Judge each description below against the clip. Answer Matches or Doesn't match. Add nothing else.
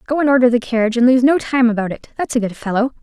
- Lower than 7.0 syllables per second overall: Doesn't match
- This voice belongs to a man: Doesn't match